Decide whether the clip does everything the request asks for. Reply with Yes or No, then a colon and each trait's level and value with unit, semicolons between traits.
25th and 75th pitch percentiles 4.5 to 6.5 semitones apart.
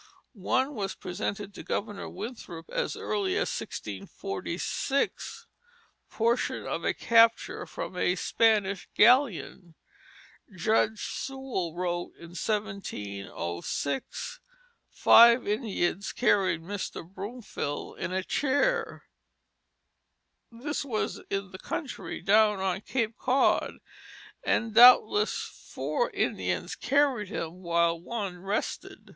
Yes: average, 5.2 semitones